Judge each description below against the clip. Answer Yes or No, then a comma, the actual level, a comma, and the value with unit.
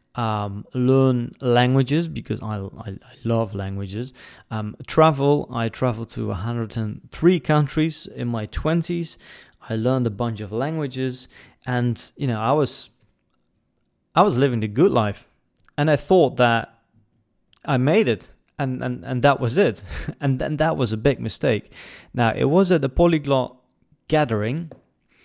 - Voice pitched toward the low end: Yes, low, 125 Hz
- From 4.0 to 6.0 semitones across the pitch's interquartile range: Yes, average, 4.3 semitones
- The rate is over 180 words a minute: No, average, 150 wpm